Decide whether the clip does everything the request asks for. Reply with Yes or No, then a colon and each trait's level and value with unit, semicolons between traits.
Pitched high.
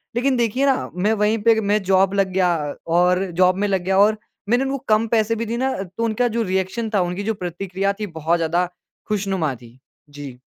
Yes: high, 200 Hz